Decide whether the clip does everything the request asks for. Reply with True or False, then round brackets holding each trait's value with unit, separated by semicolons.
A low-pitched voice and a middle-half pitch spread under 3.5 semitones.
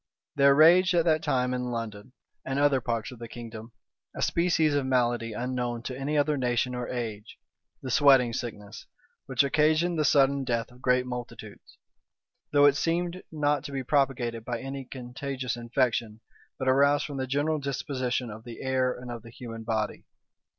True (130 Hz; 3.1 semitones)